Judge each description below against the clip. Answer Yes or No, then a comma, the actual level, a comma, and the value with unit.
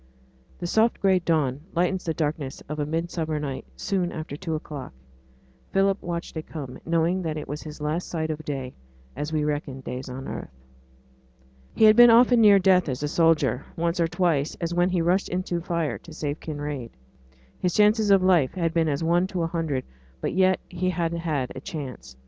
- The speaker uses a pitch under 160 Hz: No, medium, 165 Hz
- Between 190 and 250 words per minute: Yes, average, 195 wpm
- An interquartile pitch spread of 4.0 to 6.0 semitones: No, average, 3.4 semitones